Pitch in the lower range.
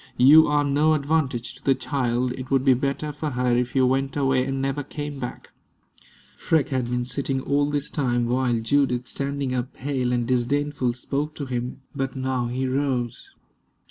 Yes: low, 130 Hz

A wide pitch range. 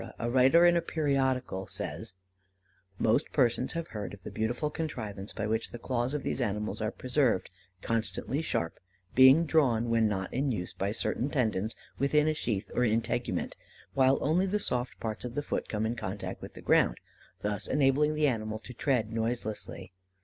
No: average, 4.4 semitones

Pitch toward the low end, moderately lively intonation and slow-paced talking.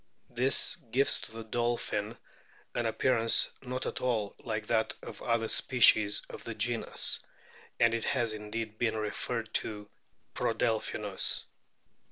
No: low, 115 Hz; narrow, 1.8 semitones; slow, 130 wpm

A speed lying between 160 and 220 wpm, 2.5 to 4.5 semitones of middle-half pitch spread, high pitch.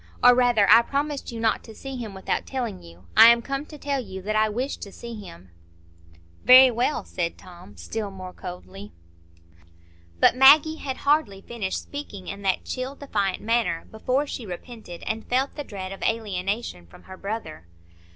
No: average, 180 wpm; average, 5.1 semitones; high, 225 Hz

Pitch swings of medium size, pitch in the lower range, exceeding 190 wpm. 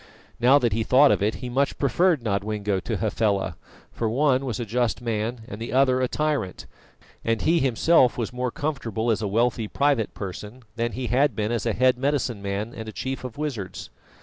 Yes: average, 3.5 semitones; low, 120 Hz; fast, 205 wpm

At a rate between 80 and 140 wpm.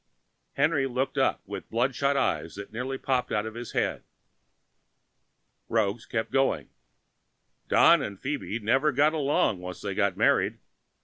Yes: slow, 135 wpm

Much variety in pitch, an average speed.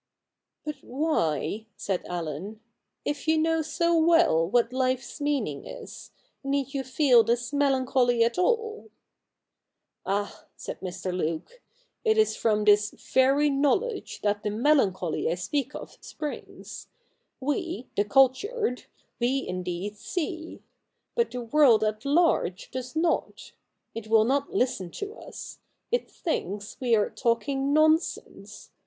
Yes: wide, 6.7 semitones; average, 150 wpm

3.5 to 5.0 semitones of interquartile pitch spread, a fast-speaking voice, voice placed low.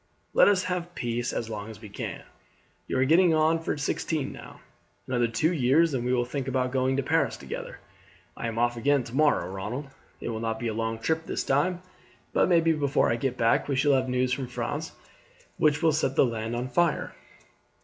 Yes: average, 4.5 semitones; fast, 210 wpm; low, 130 Hz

